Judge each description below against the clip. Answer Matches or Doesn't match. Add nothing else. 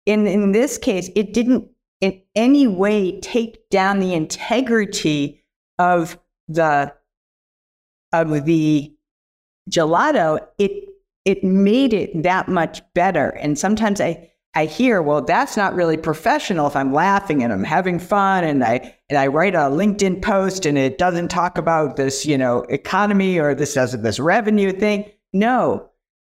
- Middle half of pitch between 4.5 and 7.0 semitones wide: Matches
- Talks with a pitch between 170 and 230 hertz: Matches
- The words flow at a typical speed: Matches